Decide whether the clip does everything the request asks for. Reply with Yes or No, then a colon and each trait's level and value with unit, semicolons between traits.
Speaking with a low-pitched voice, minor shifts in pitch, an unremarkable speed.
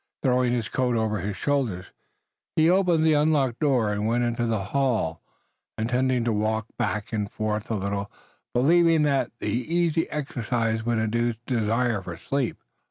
No: low, 120 Hz; average, 4.2 semitones; average, 160 wpm